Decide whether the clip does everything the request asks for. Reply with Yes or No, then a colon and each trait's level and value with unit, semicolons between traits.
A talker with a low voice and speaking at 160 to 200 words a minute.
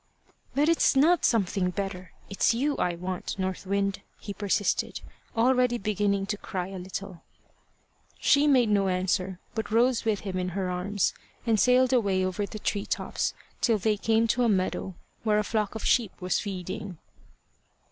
No: high, 200 Hz; average, 165 wpm